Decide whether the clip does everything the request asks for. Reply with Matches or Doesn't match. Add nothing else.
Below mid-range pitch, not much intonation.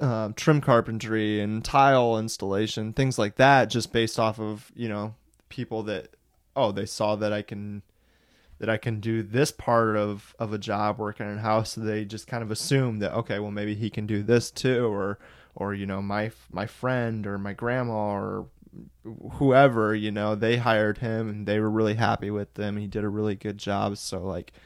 Matches